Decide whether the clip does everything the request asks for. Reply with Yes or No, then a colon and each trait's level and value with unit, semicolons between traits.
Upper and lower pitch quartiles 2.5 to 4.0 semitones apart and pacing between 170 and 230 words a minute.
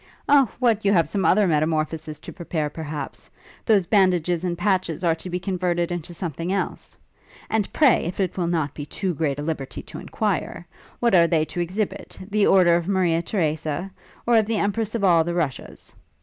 Yes: average, 3.6 semitones; average, 190 wpm